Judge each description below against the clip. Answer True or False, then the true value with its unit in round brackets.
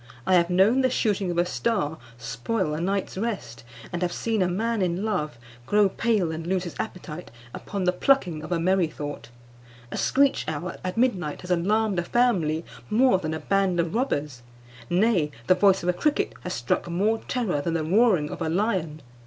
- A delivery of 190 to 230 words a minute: True (195 wpm)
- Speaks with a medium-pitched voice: True (180 Hz)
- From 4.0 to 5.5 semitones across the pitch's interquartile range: True (4.7 semitones)